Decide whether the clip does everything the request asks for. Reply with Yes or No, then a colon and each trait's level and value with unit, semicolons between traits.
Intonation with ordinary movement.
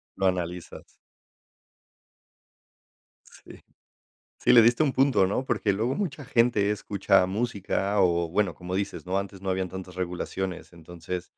Yes: average, 3.4 semitones